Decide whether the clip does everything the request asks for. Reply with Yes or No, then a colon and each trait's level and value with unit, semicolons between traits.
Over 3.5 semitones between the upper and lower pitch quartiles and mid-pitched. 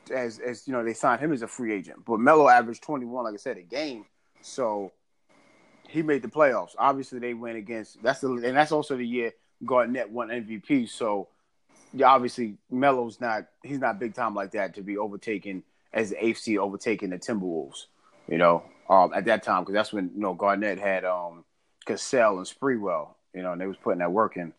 No: average, 3.9 semitones; low, 110 Hz